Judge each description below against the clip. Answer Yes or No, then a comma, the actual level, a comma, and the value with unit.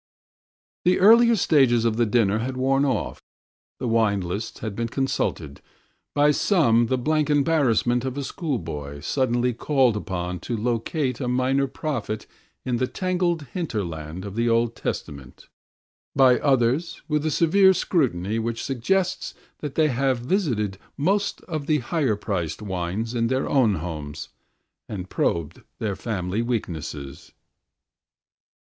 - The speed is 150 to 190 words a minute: No, average, 140 wpm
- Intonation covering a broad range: Yes, wide, 5.7 semitones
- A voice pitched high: No, low, 120 Hz